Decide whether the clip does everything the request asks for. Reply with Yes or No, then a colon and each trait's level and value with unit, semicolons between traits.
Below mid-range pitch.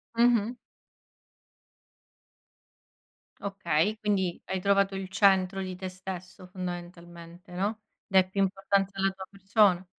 No: high, 190 Hz